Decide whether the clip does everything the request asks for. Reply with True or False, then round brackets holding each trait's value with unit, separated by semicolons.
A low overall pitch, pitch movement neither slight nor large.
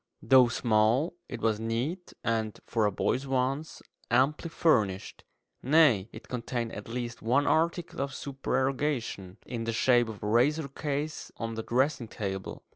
True (125 Hz; 3.8 semitones)